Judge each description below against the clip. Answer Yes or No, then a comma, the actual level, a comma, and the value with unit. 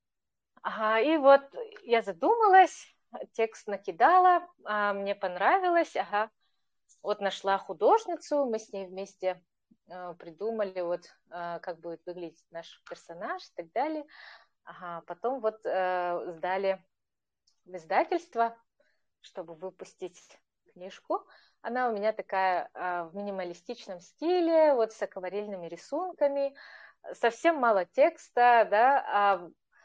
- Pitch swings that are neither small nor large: No, wide, 7.4 semitones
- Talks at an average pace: No, slow, 105 wpm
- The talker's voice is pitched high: Yes, high, 205 Hz